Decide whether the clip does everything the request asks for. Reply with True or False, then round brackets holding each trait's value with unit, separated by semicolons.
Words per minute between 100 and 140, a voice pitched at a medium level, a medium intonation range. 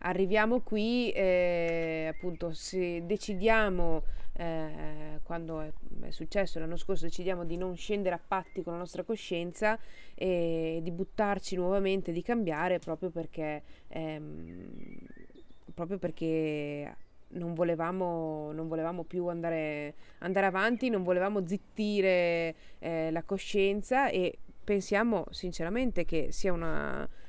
True (120 wpm; 175 Hz; 3.3 semitones)